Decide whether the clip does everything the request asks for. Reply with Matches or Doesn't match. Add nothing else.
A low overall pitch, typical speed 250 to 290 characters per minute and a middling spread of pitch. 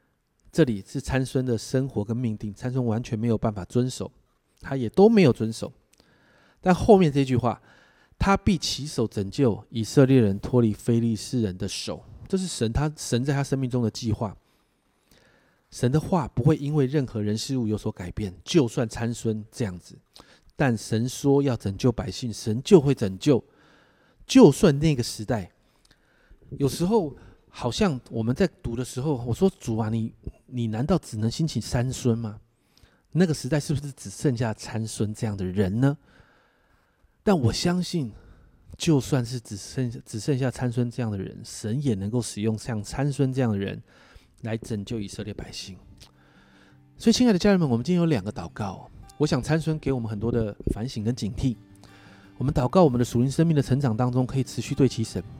Matches